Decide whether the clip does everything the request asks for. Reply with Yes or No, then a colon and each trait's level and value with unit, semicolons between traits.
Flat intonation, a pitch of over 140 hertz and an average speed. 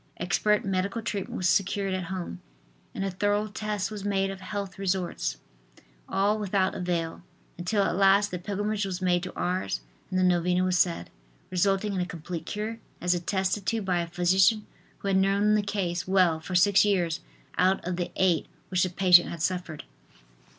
Yes: narrow, 2.1 semitones; high, 190 Hz; average, 180 wpm